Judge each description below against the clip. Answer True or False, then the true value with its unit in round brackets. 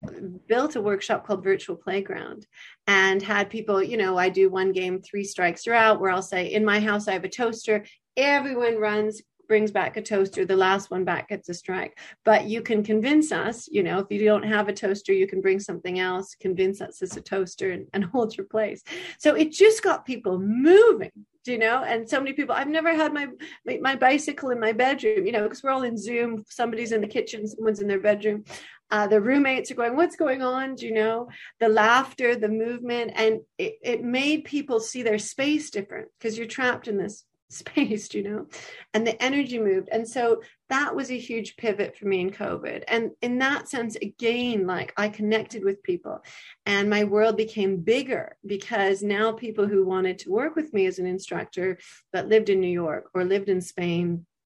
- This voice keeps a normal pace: False (210 wpm)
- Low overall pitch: False (215 Hz)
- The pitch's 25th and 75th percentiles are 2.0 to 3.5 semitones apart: False (3.9 semitones)